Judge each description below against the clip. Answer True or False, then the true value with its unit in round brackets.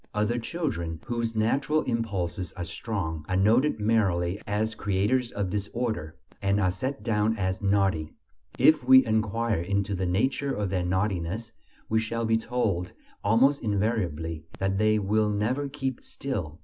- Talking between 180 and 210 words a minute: False (150 wpm)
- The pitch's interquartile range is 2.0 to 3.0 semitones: False (3.7 semitones)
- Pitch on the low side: True (105 Hz)